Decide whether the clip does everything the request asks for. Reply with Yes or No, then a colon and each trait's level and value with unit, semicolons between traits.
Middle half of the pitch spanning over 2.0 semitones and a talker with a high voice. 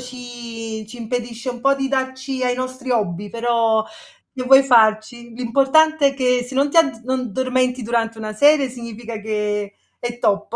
Yes: narrow, 2.6 semitones; high, 245 Hz